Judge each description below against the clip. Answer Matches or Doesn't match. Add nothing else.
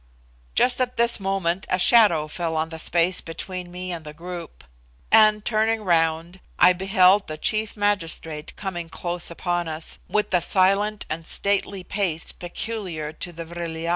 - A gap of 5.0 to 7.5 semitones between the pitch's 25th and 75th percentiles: Doesn't match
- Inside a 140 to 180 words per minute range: Matches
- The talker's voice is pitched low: Doesn't match